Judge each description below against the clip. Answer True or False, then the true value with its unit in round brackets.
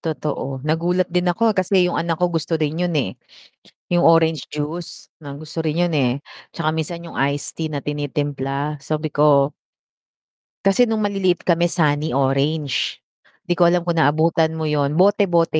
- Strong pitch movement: False (2.9 semitones)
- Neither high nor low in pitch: True (160 Hz)